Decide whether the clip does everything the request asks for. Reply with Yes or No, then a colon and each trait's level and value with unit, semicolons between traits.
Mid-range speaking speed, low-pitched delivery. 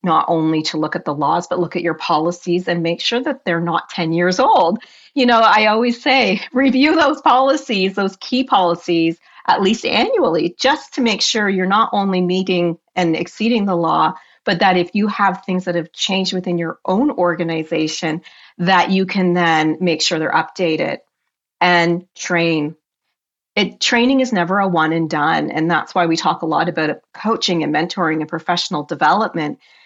No: average, 185 wpm; medium, 180 Hz